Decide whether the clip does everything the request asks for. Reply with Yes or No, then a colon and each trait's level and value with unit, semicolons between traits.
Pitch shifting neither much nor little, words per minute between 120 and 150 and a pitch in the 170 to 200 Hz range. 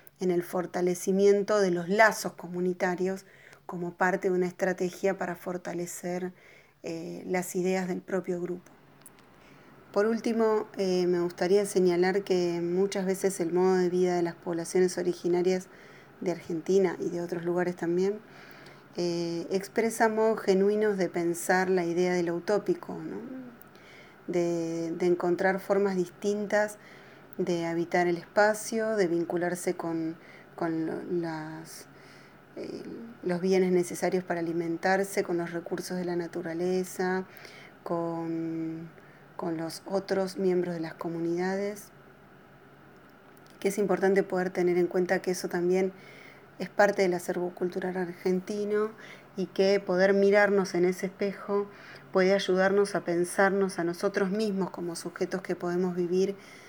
No: narrow, 1.9 semitones; average, 130 wpm; medium, 185 Hz